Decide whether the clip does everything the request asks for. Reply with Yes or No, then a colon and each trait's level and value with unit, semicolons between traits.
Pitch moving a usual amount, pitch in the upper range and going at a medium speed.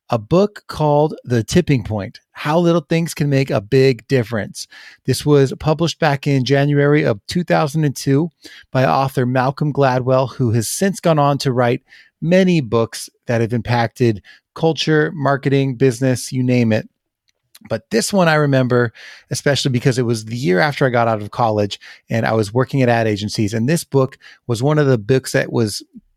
No: average, 3.9 semitones; low, 135 Hz; average, 180 wpm